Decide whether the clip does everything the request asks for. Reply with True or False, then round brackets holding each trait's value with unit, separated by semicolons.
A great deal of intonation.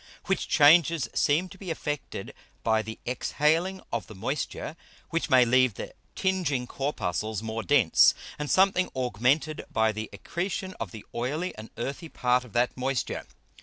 True (6.0 semitones)